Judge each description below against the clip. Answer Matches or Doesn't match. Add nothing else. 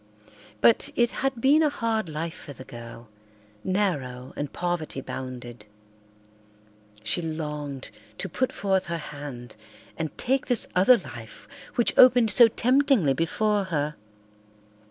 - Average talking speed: Doesn't match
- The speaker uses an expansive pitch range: Matches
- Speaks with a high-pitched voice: Doesn't match